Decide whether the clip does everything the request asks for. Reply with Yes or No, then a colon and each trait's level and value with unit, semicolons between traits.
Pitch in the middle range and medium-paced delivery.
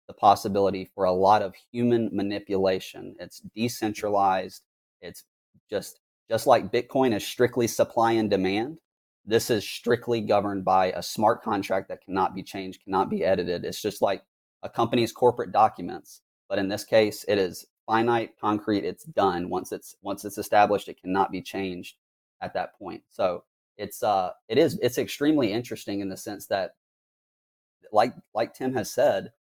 No: low, 105 Hz; average, 165 wpm